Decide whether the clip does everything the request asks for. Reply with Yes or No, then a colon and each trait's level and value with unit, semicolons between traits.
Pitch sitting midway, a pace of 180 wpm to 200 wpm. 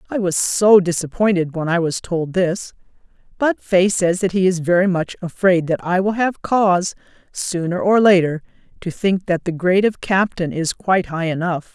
Yes: medium, 180 Hz; average, 190 wpm